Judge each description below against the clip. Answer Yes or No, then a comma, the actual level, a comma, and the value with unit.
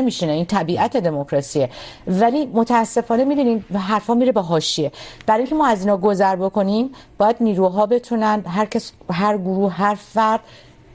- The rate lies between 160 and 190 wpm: No, average, 150 wpm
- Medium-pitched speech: No, high, 210 Hz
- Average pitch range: Yes, average, 3.6 semitones